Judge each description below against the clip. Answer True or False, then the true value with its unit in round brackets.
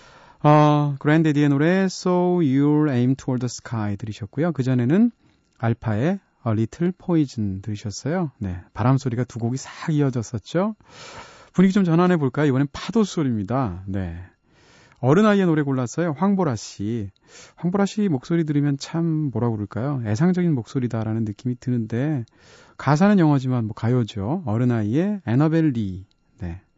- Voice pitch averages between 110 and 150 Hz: True (140 Hz)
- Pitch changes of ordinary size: False (6.7 semitones)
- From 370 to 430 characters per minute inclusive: True (375 characters per minute)